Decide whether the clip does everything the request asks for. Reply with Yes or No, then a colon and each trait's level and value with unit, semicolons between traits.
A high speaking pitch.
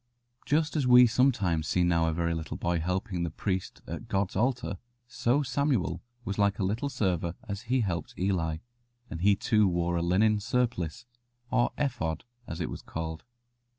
No: very low, 95 Hz